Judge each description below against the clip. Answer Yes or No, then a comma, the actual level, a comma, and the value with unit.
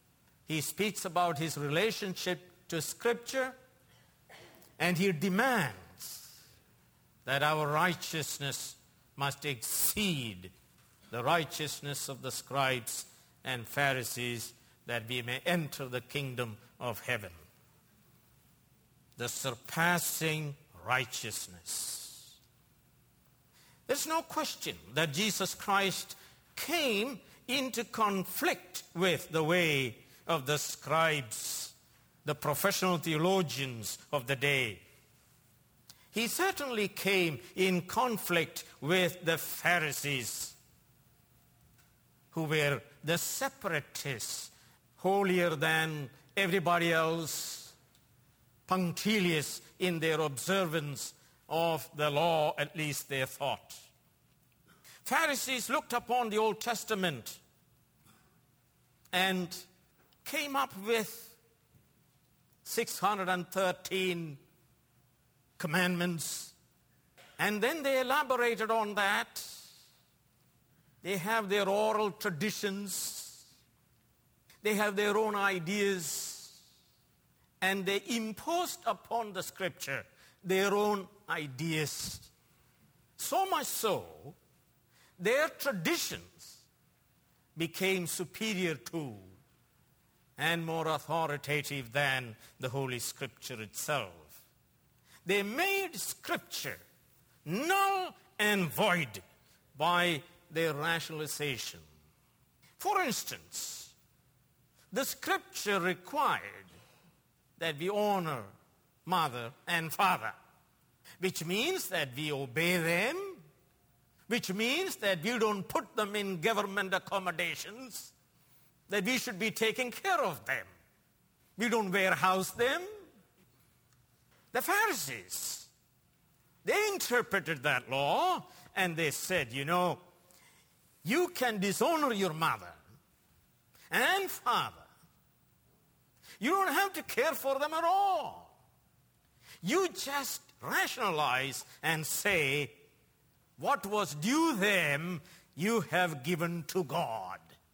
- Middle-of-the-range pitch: Yes, medium, 175 Hz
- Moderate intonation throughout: No, wide, 6.5 semitones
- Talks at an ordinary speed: No, slow, 90 wpm